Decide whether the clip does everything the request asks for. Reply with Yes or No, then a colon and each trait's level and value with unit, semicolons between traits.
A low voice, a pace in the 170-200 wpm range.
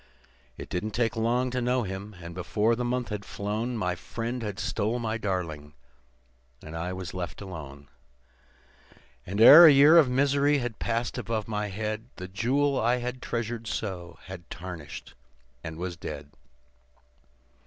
No: low, 110 Hz; average, 155 wpm